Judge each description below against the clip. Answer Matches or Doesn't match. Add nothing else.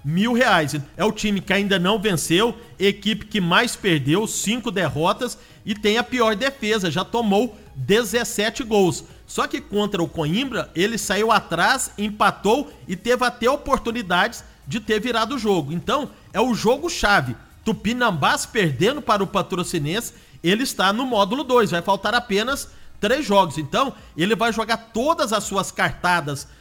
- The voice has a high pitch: Matches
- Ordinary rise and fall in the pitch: Matches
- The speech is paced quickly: Doesn't match